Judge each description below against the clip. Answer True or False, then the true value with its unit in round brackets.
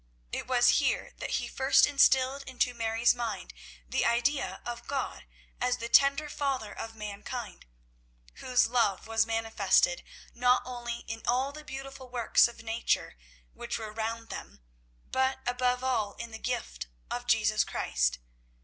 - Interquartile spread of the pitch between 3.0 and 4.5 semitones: False (2.5 semitones)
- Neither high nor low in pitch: False (240 Hz)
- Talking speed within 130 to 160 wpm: True (150 wpm)